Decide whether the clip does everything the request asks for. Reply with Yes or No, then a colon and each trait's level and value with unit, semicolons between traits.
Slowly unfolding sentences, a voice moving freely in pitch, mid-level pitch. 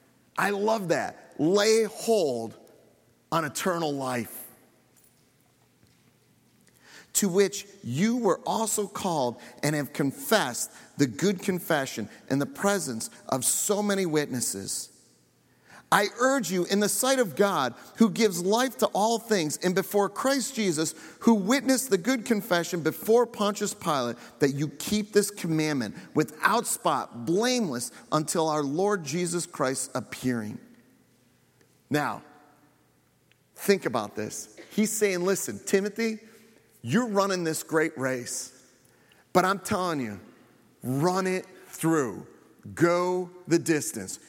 Yes: slow, 120 wpm; wide, 7.7 semitones; medium, 180 Hz